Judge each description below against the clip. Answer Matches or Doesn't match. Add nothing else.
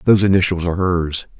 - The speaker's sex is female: Doesn't match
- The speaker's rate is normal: Matches